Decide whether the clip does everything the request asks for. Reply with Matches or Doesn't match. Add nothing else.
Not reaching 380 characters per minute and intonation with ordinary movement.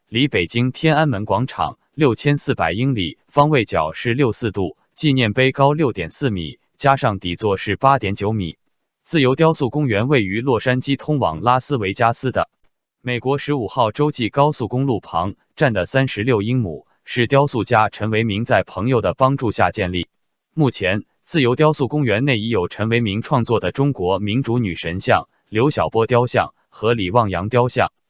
Matches